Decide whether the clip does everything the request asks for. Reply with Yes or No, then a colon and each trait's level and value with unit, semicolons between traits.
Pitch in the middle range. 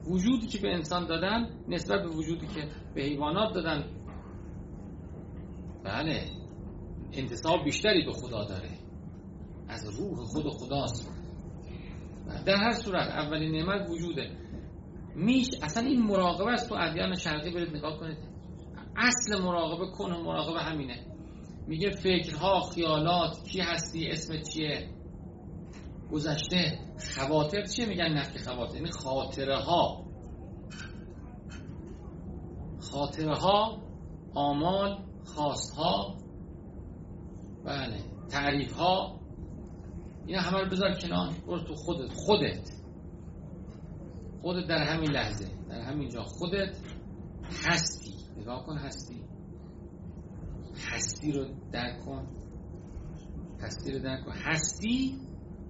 Yes: medium, 150 Hz